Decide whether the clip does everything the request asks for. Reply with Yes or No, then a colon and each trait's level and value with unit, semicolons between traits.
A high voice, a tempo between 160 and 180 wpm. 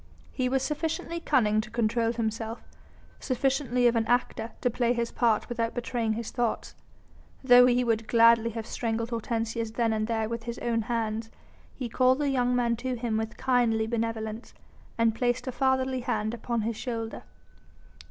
Yes: high, 235 Hz; average, 170 wpm